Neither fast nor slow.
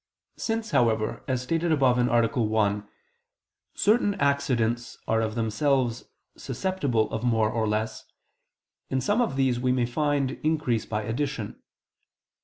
No: slow, 130 wpm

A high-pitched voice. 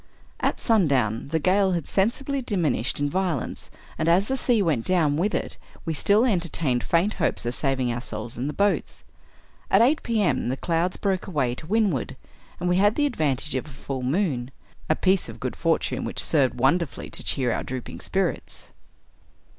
No: medium, 165 Hz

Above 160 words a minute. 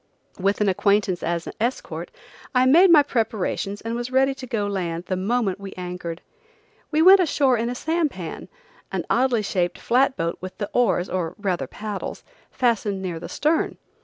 Yes: average, 175 wpm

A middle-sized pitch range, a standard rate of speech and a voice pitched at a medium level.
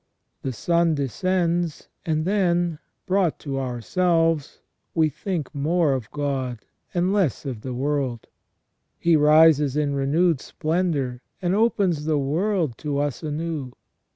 No: average, 4.0 semitones; slow, 125 wpm; medium, 155 Hz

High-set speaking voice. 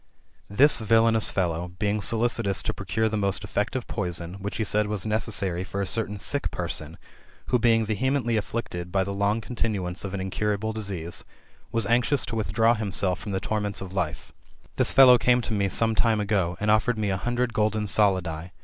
No: low, 105 Hz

